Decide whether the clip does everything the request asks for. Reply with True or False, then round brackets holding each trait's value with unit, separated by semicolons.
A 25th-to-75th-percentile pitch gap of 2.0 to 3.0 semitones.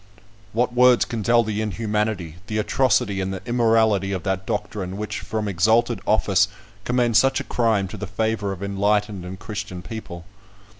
True (2.7 semitones)